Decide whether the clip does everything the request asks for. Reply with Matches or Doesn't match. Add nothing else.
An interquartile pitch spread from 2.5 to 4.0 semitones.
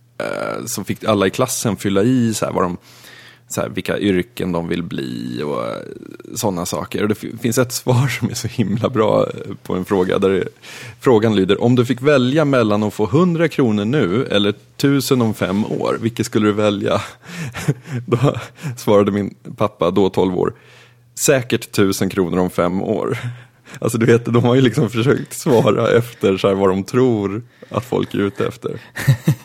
Matches